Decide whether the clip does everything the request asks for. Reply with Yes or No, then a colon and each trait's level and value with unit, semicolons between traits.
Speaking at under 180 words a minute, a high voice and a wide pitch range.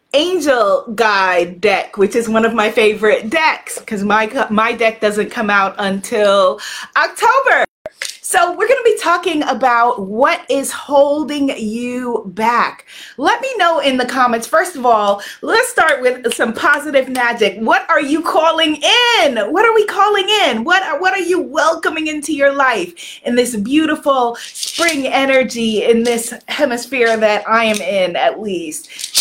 Yes: average, 160 wpm; very high, 270 Hz; wide, 6.2 semitones